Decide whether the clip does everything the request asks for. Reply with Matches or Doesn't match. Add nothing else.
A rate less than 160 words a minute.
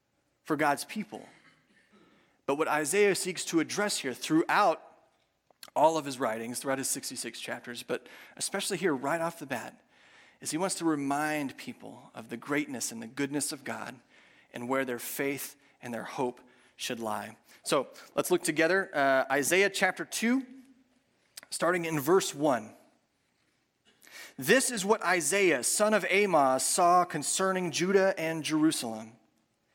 Matches